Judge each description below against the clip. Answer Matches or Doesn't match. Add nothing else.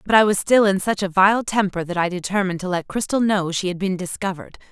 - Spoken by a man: Doesn't match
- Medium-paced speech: Doesn't match